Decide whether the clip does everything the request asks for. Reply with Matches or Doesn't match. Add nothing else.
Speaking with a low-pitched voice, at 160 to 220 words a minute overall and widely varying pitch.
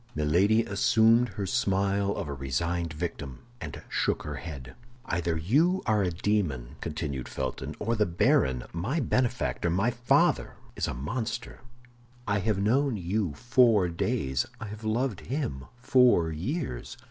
Doesn't match